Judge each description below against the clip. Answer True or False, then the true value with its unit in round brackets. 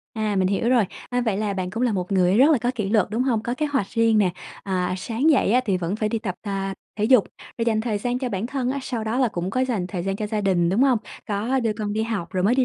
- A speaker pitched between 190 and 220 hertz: True (215 Hz)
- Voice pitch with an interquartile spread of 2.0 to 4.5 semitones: True (3.9 semitones)